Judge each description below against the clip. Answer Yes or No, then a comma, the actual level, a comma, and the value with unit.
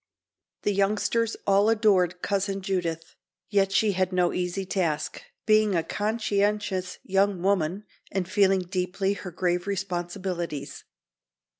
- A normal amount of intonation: No, narrow, 2.1 semitones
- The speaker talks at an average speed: No, slow, 120 wpm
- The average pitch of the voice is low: No, high, 195 Hz